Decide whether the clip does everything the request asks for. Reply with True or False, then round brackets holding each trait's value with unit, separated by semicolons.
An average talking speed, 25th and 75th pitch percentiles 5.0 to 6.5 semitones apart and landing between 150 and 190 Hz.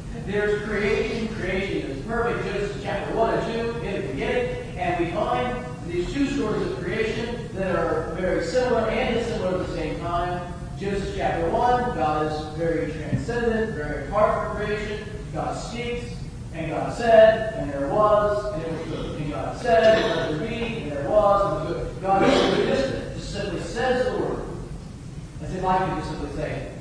True (190 wpm; 5.3 semitones; 185 Hz)